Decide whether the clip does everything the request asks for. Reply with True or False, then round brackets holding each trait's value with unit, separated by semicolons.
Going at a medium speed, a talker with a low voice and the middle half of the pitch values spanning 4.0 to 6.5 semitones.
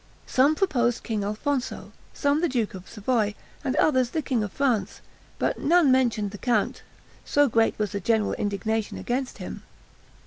False (165 wpm; 240 Hz; 4.5 semitones)